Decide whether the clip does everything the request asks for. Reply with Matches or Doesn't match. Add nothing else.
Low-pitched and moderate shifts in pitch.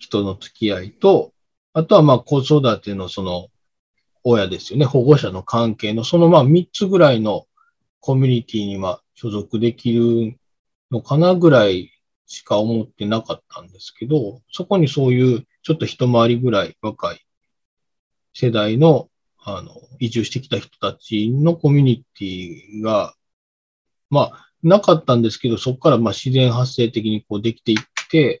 Matches